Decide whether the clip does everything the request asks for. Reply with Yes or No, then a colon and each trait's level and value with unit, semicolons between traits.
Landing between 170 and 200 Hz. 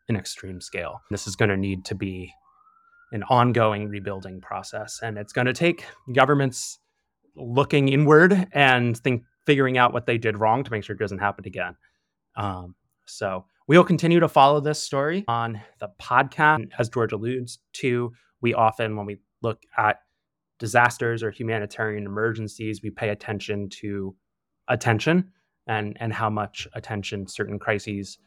No: low, 115 Hz